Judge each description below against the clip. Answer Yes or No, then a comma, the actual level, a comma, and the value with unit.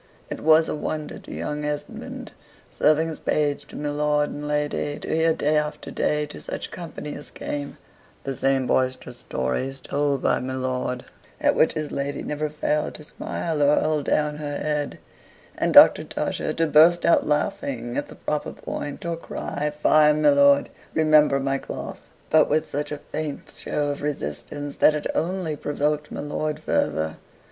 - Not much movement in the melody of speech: Yes, narrow, 1.3 semitones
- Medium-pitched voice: Yes, medium, 150 Hz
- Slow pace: No, average, 175 wpm